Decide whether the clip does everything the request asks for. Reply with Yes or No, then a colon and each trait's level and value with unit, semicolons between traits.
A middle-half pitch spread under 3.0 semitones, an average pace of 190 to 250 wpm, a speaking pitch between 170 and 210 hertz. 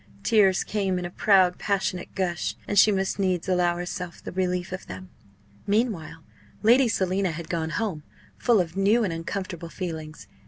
No: narrow, 2.5 semitones; average, 165 wpm; medium, 185 Hz